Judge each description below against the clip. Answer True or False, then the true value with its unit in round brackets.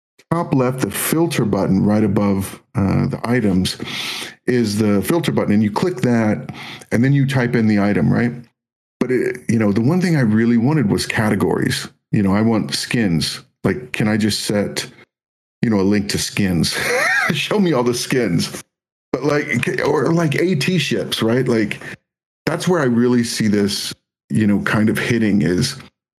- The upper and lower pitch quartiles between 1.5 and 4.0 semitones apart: False (4.7 semitones)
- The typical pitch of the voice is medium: False (120 Hz)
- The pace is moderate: True (180 wpm)